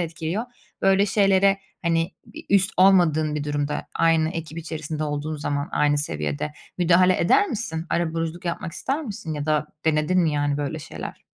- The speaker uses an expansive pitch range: No, average, 3.4 semitones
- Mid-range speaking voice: Yes, medium, 160 Hz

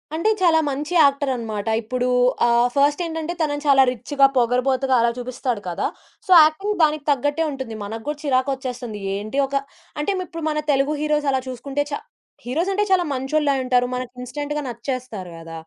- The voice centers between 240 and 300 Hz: Yes, very high, 270 Hz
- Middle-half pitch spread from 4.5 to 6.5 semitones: No, average, 3.3 semitones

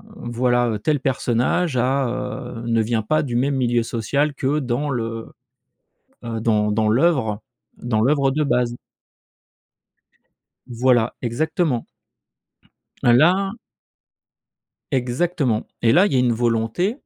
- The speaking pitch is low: Yes, low, 125 Hz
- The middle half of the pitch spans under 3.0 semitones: No, average, 3.6 semitones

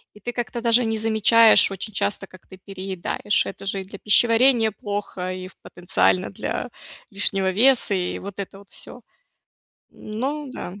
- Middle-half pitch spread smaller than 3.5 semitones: Yes, average, 3.0 semitones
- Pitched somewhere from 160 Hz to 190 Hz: No, high, 205 Hz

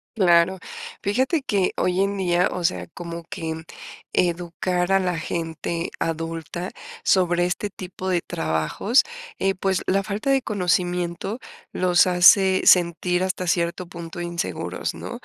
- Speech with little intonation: Yes, narrow, 2.0 semitones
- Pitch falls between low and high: Yes, medium, 180 Hz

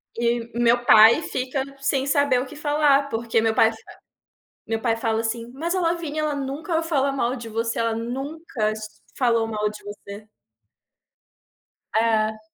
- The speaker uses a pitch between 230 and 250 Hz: Yes, high, 240 Hz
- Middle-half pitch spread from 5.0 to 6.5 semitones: No, average, 4.0 semitones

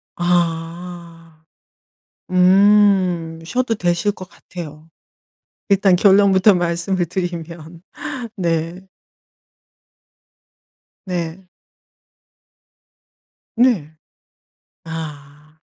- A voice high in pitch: No, medium, 175 Hz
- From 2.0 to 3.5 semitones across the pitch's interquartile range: Yes, narrow, 2.6 semitones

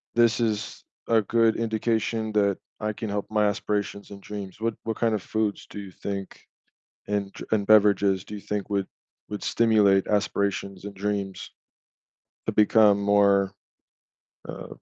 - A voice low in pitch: Yes, low, 105 Hz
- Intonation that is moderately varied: No, narrow, 1.6 semitones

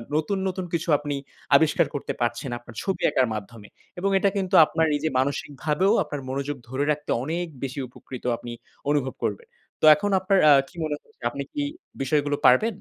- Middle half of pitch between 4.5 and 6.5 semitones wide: Yes, average, 5.0 semitones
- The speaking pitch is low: No, medium, 145 Hz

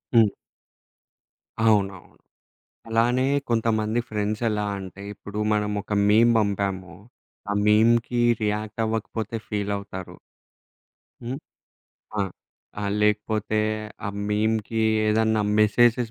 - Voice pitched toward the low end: Yes, low, 105 Hz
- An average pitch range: No, narrow, 1.5 semitones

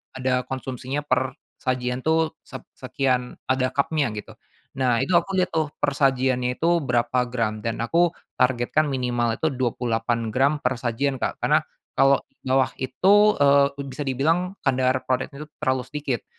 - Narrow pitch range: Yes, narrow, 2.3 semitones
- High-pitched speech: No, low, 130 Hz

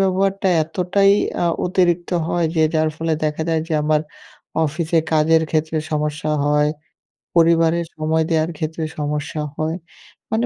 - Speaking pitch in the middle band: Yes, medium, 160 Hz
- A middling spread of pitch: No, narrow, 1.8 semitones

